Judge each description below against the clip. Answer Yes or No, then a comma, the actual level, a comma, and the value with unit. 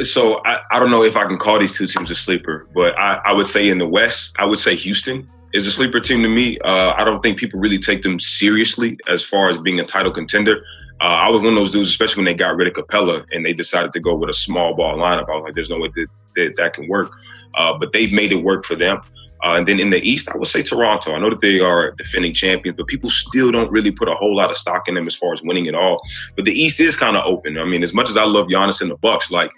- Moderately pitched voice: No, low, 100 Hz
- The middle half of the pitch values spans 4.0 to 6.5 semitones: No, average, 3.3 semitones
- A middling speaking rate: No, fast, 295 wpm